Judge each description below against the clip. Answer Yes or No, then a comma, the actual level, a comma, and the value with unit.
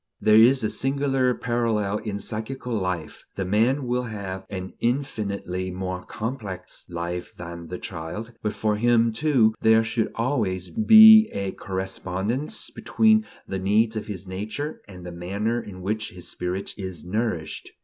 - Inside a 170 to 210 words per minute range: No, average, 150 wpm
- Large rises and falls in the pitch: No, average, 4.4 semitones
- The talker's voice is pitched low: Yes, low, 105 Hz